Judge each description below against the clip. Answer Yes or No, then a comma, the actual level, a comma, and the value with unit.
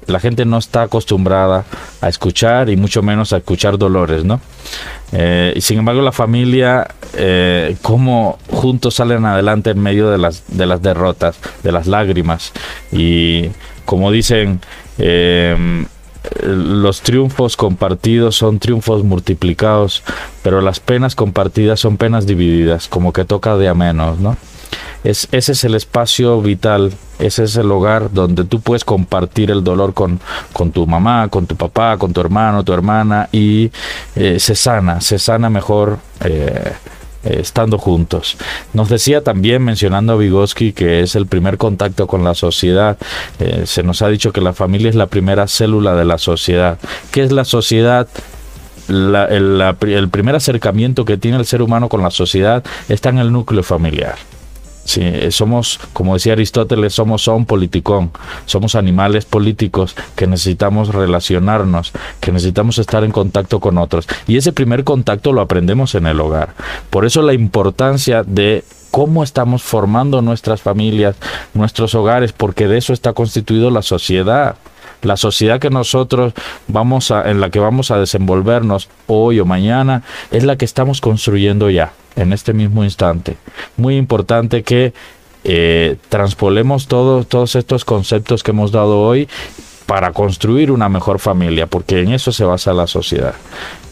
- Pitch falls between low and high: No, low, 105 Hz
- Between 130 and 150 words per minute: No, average, 160 wpm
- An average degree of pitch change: Yes, average, 3.8 semitones